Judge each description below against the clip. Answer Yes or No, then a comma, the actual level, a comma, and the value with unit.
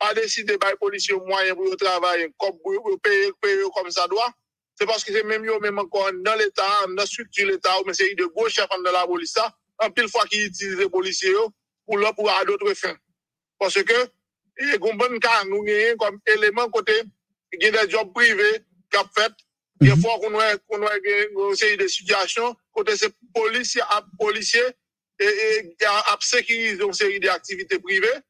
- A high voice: Yes, high, 215 Hz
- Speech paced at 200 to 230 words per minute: Yes, average, 210 wpm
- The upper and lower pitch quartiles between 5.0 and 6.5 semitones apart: No, average, 3.9 semitones